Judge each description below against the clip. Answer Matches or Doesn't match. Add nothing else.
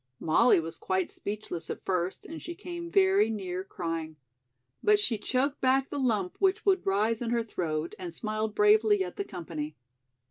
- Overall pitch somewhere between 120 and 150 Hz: Doesn't match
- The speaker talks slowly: Doesn't match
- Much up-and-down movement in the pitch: Matches